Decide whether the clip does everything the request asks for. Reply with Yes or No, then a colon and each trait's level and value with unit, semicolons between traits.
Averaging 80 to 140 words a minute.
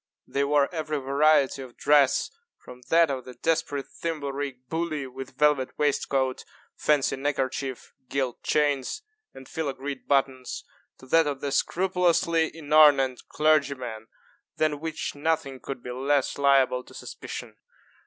Yes: slow, 135 wpm